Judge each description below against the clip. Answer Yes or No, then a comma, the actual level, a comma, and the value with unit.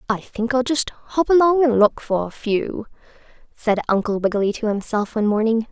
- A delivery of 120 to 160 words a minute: No, average, 190 wpm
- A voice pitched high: Yes, high, 230 Hz